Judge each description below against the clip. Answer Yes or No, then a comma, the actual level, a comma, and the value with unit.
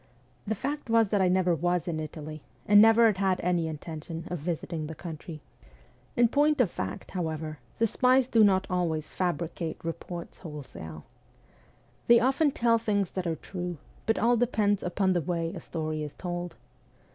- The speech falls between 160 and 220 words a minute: Yes, average, 175 wpm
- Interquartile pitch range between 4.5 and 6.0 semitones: Yes, average, 5.1 semitones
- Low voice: No, medium, 175 Hz